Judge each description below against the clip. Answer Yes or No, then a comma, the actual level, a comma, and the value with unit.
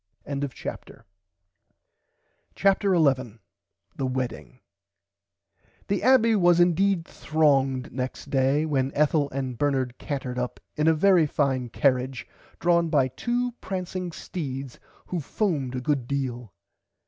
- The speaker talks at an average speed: No, slow, 120 wpm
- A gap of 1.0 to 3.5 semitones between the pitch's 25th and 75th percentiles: No, average, 5.1 semitones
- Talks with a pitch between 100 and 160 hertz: Yes, medium, 140 Hz